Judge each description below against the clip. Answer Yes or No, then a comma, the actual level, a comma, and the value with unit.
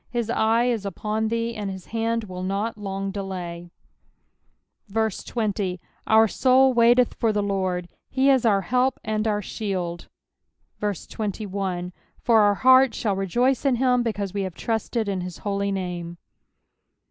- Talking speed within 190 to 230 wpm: No, average, 145 wpm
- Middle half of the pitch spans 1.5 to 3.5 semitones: Yes, average, 3.1 semitones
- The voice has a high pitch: Yes, high, 210 Hz